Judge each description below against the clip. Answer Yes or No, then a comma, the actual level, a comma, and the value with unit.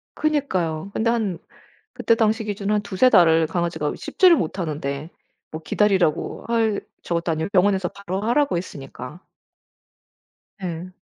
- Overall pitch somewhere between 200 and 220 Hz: No, medium, 185 Hz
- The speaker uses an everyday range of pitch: Yes, average, 4.7 semitones